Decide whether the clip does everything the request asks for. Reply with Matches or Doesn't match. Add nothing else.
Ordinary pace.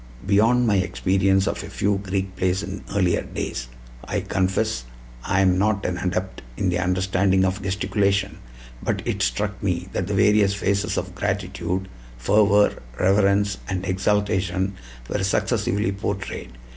Matches